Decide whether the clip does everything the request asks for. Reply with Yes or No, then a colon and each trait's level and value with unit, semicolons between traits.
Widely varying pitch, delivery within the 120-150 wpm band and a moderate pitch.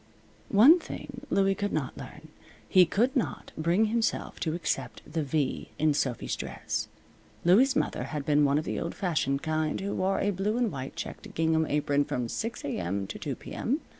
No: wide, 6.3 semitones; average, 185 wpm; medium, 165 Hz